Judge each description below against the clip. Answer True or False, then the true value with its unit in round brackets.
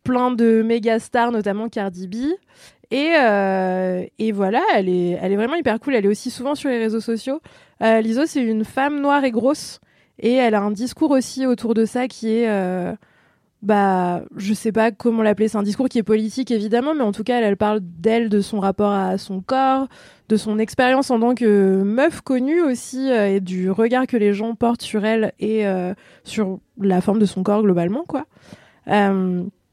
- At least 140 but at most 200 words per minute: False (210 wpm)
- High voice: True (225 Hz)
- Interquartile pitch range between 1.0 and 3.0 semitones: False (3.6 semitones)